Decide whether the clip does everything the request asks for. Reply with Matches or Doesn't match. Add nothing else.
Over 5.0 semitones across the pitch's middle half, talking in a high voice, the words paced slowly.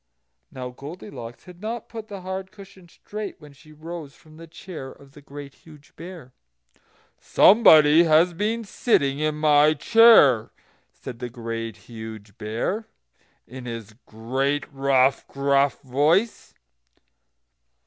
Doesn't match